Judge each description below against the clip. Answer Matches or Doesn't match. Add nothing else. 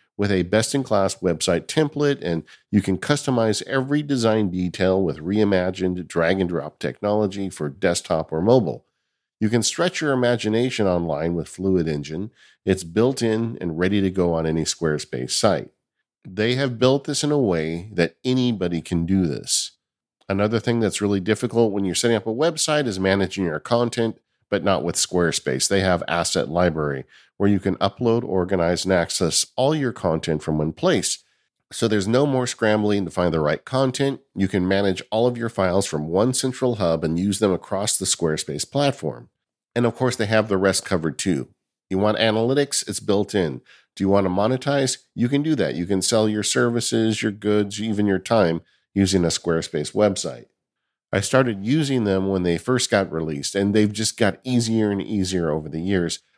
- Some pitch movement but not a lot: Matches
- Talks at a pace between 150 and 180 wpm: Doesn't match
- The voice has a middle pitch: Doesn't match